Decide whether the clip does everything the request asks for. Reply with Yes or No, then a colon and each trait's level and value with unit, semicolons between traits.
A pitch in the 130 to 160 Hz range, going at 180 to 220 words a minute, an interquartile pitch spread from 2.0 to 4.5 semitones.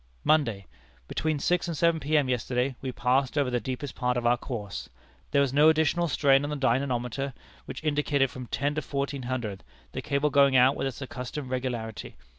Yes: low, 135 Hz; average, 190 wpm; average, 2.7 semitones